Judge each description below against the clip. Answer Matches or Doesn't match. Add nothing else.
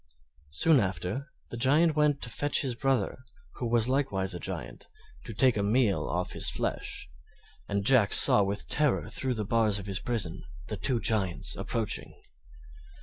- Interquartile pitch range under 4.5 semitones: Doesn't match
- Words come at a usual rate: Matches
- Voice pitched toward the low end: Matches